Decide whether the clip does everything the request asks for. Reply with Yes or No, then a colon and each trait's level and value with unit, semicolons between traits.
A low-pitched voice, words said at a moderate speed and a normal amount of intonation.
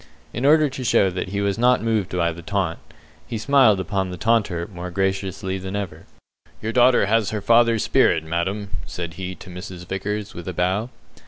Yes: low, 100 Hz; average, 190 wpm; average, 3.7 semitones